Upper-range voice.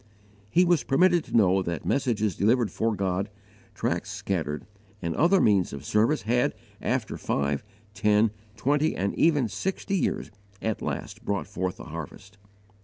No: low, 105 Hz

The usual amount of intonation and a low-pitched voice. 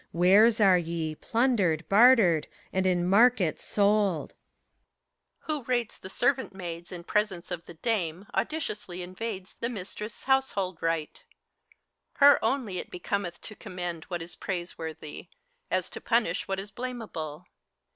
No: average, 4.6 semitones; high, 190 Hz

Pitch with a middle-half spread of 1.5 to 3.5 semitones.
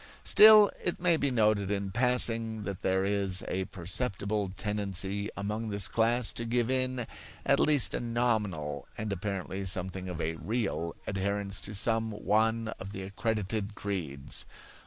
Yes: average, 3.1 semitones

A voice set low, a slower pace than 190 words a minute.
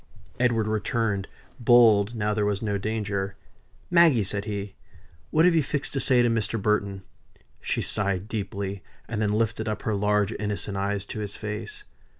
Yes: low, 105 Hz; average, 165 wpm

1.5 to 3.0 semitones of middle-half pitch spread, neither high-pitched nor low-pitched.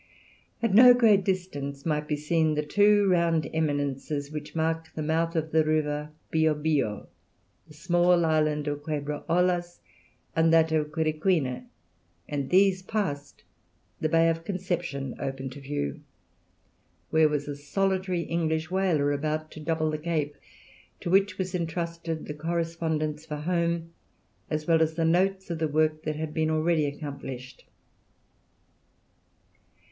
Yes: narrow, 2.4 semitones; medium, 160 Hz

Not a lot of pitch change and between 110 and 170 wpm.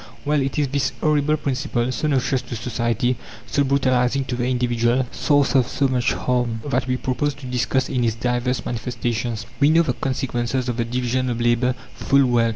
No: narrow, 2.2 semitones; average, 190 wpm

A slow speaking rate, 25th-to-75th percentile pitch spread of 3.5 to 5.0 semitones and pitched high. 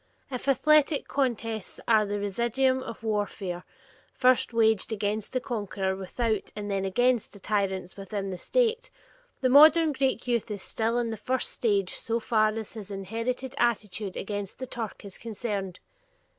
No: average, 160 wpm; average, 3.8 semitones; high, 220 Hz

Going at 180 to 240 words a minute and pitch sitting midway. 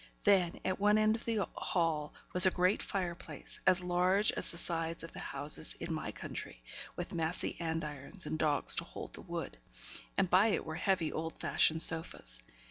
Yes: average, 190 wpm; medium, 170 Hz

